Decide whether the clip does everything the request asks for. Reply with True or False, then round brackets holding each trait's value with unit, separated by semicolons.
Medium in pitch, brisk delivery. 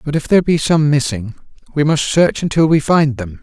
True (145 Hz; 230 wpm)